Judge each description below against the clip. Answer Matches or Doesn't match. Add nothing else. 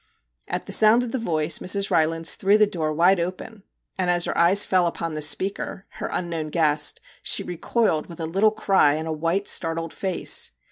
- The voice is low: Doesn't match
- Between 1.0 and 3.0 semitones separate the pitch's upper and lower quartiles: Doesn't match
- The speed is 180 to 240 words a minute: Matches